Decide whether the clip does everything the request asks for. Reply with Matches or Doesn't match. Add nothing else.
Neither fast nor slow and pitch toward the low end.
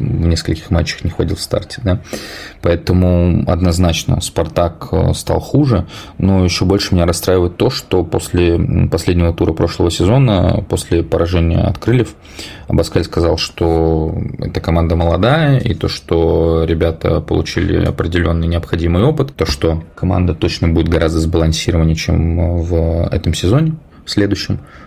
Matches